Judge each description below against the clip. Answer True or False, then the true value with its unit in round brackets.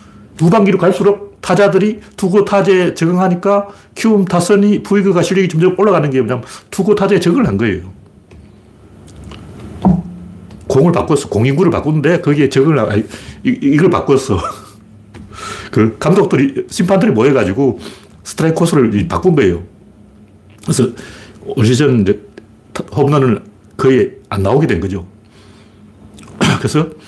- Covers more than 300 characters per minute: False (285 characters per minute)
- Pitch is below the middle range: False (150 Hz)